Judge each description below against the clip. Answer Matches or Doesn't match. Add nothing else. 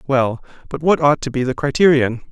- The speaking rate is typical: Doesn't match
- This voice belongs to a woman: Doesn't match